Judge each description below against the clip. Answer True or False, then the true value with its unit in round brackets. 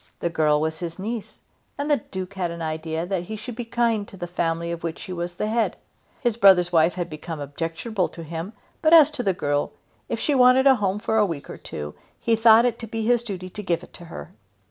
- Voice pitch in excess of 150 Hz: True (185 Hz)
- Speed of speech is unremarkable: False (245 wpm)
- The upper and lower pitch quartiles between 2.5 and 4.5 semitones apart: False (5.3 semitones)